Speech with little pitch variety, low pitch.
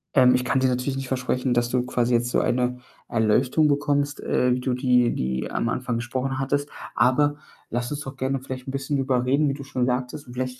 Yes: narrow, 1.6 semitones; low, 130 Hz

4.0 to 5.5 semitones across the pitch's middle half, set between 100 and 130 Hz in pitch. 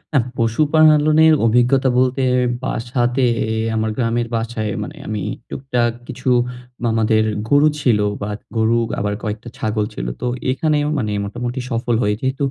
No: average, 3.1 semitones; low, 120 Hz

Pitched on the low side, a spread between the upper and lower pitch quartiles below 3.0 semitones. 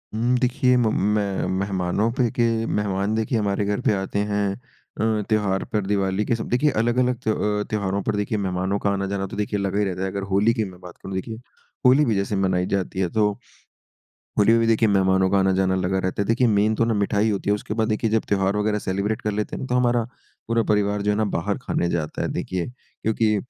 Yes: low, 105 Hz; narrow, 2.4 semitones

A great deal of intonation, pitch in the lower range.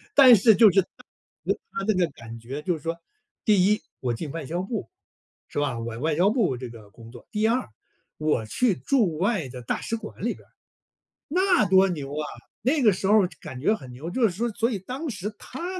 No: wide, 8.0 semitones; medium, 185 Hz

